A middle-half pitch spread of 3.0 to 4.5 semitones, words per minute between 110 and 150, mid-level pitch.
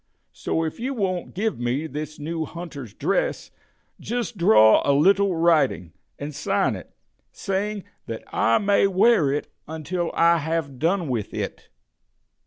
No: wide, 5.5 semitones; average, 145 wpm; medium, 165 Hz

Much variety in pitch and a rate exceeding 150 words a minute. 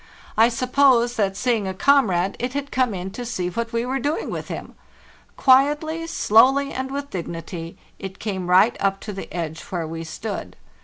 Yes: wide, 5.9 semitones; average, 185 wpm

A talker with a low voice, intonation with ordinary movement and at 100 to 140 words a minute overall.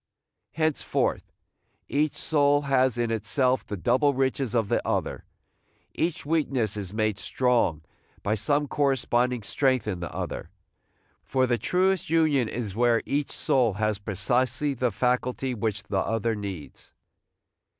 Yes: low, 125 Hz; average, 4.5 semitones; slow, 135 wpm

